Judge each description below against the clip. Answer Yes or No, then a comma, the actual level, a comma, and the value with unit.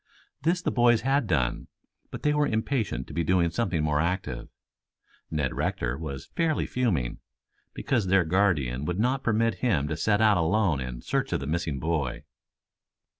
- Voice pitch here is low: Yes, very low, 90 Hz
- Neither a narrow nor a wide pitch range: No, wide, 7.6 semitones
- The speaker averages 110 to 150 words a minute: No, average, 170 wpm